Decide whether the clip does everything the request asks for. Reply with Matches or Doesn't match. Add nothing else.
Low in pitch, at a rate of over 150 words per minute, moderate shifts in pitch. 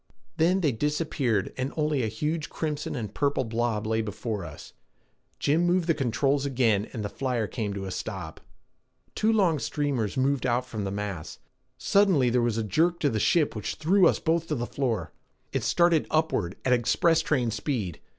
Doesn't match